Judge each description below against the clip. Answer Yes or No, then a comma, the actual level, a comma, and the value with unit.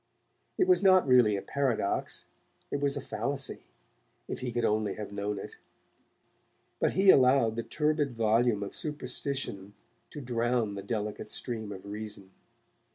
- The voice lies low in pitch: Yes, low, 115 Hz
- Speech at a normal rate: Yes, average, 150 wpm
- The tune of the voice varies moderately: Yes, average, 4.9 semitones